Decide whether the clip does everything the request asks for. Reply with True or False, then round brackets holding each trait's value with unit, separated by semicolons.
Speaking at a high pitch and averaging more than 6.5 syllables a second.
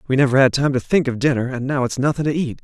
False (135 Hz; 6.9 syllables/s)